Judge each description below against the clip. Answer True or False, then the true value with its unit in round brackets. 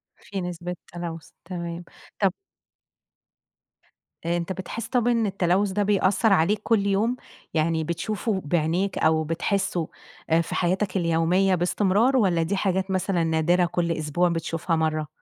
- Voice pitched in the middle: True (180 Hz)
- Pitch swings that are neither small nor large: True (3.0 semitones)